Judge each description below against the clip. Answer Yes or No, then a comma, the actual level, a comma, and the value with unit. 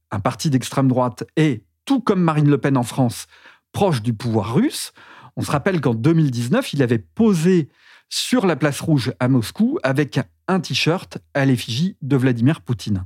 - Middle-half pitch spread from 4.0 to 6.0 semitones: Yes, average, 4.6 semitones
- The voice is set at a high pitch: No, medium, 140 Hz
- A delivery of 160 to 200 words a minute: Yes, average, 175 wpm